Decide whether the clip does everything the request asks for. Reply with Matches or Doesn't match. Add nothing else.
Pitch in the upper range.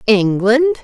Matches